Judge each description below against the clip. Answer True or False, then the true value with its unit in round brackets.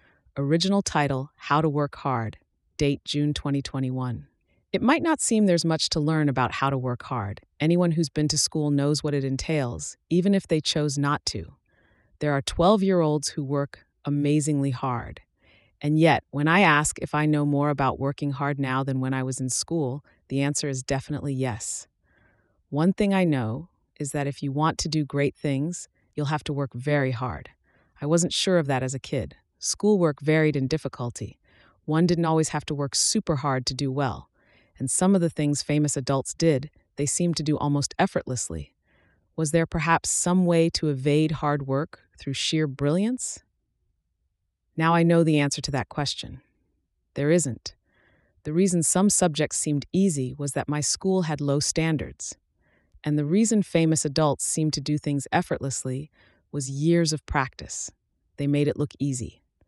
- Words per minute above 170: True (180 wpm)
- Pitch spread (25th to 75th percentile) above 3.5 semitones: False (3.1 semitones)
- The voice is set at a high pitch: False (145 Hz)